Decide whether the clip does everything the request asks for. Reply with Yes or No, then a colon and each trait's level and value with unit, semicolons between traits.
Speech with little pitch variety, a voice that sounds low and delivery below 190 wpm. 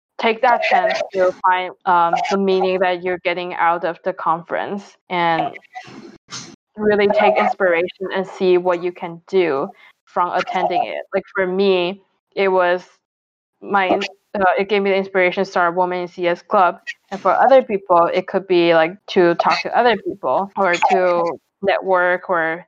No: narrow, 1.8 semitones; medium, 185 Hz; average, 170 wpm